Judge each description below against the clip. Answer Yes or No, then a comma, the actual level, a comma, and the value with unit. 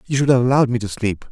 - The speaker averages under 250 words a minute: No, fast, 320 wpm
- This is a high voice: No, low, 120 Hz